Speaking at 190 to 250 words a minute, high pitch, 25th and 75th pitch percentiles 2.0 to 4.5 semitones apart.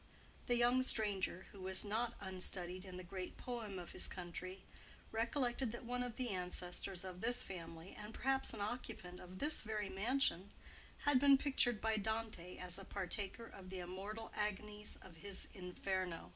No: average, 170 wpm; high, 200 Hz; average, 4.2 semitones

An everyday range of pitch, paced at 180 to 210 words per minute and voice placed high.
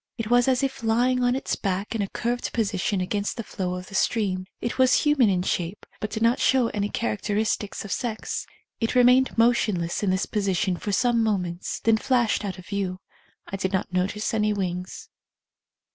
Yes: average, 4.0 semitones; average, 195 wpm; high, 210 Hz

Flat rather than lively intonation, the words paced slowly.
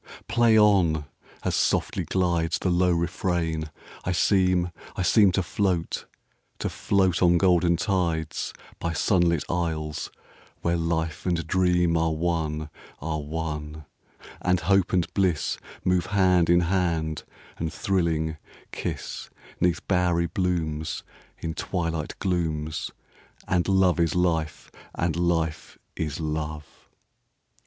Yes: narrow, 2.2 semitones; slow, 100 wpm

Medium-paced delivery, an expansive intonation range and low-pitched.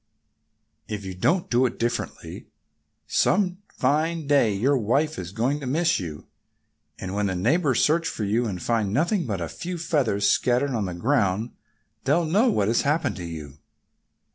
Yes: average, 165 wpm; wide, 7.5 semitones; low, 120 Hz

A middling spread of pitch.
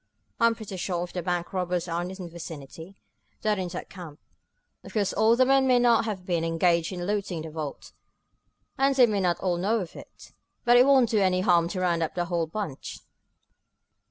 Yes: average, 3.9 semitones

